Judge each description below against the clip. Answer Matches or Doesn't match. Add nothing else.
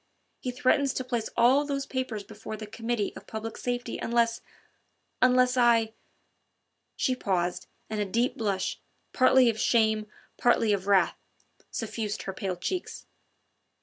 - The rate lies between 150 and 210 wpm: Doesn't match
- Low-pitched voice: Doesn't match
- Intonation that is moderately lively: Matches